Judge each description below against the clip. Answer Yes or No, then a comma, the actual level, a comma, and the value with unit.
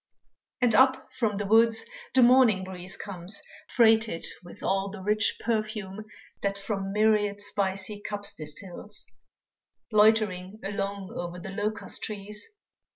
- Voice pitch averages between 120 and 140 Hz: No, high, 205 Hz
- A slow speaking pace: Yes, slow, 125 wpm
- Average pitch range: No, narrow, 2.2 semitones